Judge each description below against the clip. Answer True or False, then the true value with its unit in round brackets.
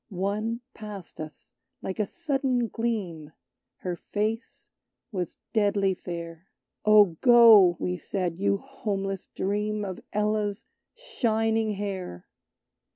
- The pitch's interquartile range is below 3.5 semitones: True (3.1 semitones)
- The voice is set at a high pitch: True (205 Hz)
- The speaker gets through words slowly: True (105 wpm)